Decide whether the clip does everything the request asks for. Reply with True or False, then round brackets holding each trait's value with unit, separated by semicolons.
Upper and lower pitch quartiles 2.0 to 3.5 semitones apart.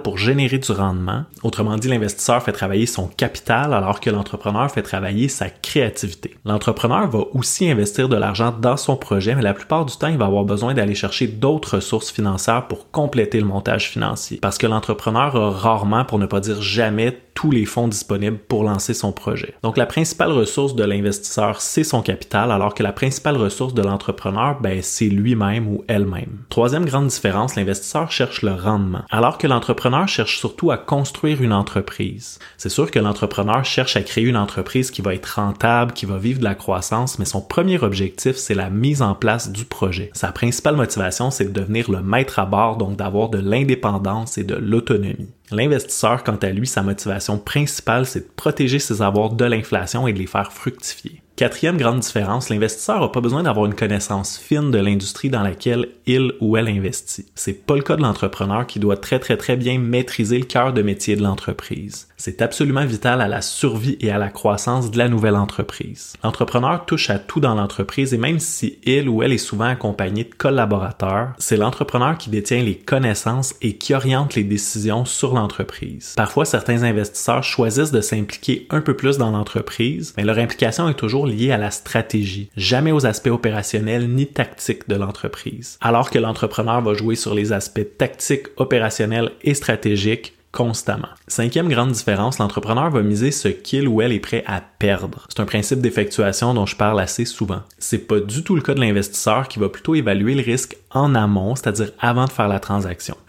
False (3.9 semitones)